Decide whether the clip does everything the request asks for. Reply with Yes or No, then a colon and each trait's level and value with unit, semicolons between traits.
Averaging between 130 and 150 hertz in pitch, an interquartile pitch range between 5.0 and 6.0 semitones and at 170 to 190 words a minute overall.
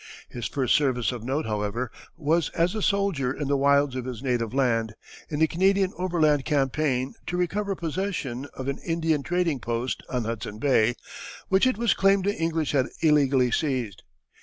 Yes: medium, 140 Hz; average, 5.3 semitones; average, 175 wpm